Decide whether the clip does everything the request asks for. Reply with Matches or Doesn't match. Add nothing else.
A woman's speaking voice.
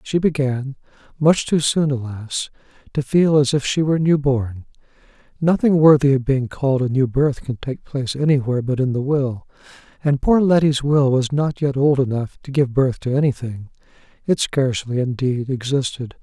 Doesn't match